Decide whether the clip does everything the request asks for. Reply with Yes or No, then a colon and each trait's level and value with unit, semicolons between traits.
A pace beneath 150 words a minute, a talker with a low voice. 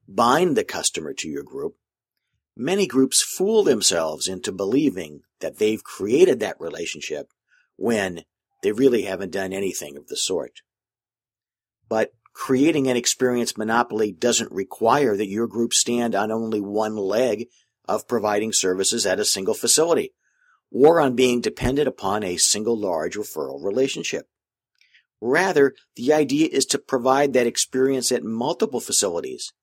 Yes: average, 140 wpm; low, 130 Hz